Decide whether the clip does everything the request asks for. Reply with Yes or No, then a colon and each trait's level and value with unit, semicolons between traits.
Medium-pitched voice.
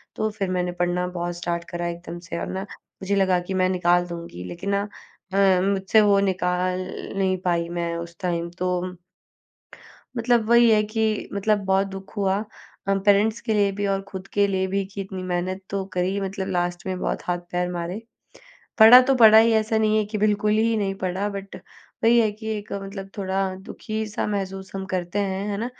No: high, 195 Hz